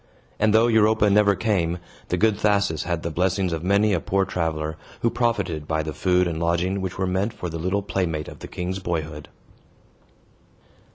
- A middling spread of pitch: Yes, average, 3.5 semitones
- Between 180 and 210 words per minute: Yes, average, 185 wpm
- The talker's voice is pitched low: Yes, very low, 90 Hz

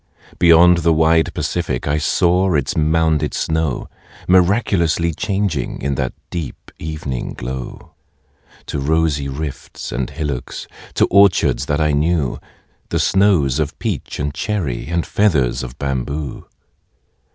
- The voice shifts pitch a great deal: No, average, 3.6 semitones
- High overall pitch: No, very low, 80 Hz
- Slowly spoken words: Yes, slow, 125 wpm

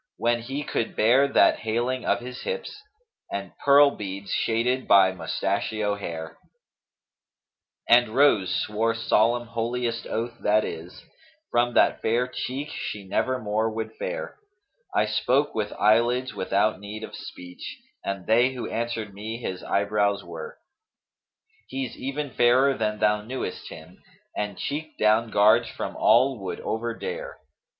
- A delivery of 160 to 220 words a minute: No, average, 145 wpm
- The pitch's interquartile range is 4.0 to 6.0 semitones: No, average, 3.5 semitones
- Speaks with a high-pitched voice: No, low, 115 Hz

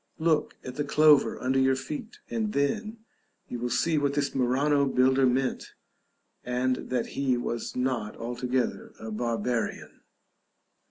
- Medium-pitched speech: No, low, 130 Hz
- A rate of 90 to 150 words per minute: Yes, average, 140 wpm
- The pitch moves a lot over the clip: No, average, 2.8 semitones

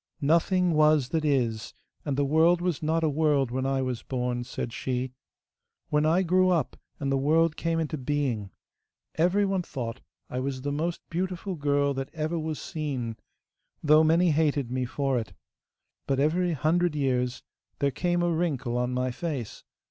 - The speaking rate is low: No, average, 170 wpm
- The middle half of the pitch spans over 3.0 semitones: Yes, average, 4.1 semitones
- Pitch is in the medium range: Yes, medium, 150 Hz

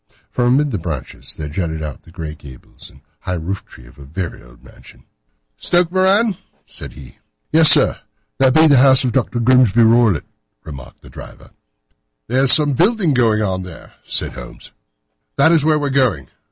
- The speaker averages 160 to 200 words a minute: Yes, average, 185 wpm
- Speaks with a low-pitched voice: Yes, low, 115 Hz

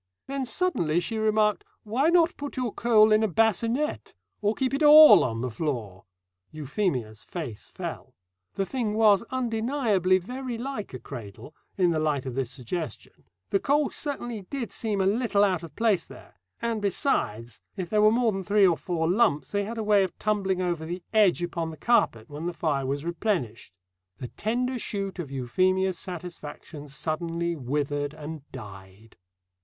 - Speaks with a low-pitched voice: No, medium, 185 Hz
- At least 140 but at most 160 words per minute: No, average, 170 wpm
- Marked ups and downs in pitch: Yes, wide, 7.0 semitones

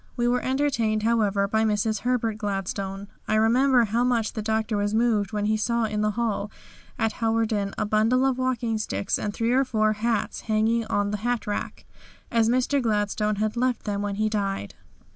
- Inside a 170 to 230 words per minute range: Yes, average, 190 wpm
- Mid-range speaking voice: No, high, 220 Hz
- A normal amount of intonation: No, narrow, 2.1 semitones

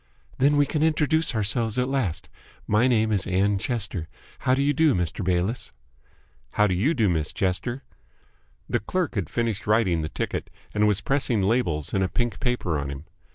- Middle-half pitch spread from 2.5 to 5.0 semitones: No, wide, 5.6 semitones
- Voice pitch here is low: Yes, low, 110 Hz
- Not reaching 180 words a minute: No, average, 185 wpm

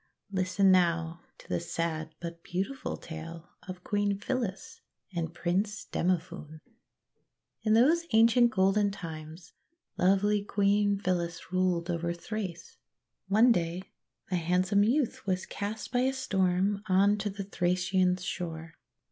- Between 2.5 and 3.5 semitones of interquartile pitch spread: Yes, average, 3.1 semitones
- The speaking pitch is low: No, medium, 185 Hz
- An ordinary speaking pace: No, slow, 125 wpm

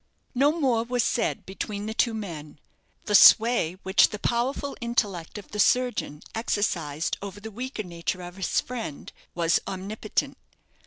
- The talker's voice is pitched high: Yes, high, 210 Hz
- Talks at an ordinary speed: Yes, average, 150 wpm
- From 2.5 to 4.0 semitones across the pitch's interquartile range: No, average, 4.7 semitones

